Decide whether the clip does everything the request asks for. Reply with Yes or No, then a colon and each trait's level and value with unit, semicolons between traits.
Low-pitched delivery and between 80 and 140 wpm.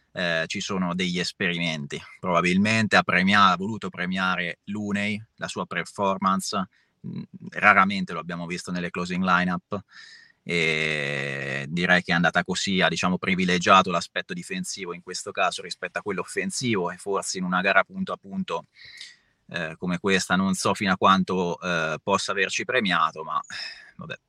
No: very low, 90 Hz; average, 155 wpm